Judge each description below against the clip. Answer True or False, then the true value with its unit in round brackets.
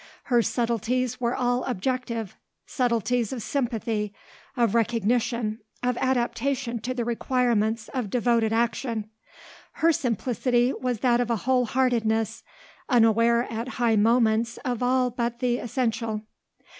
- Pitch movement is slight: True (1.8 semitones)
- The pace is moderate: False (125 wpm)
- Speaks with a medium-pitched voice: False (235 Hz)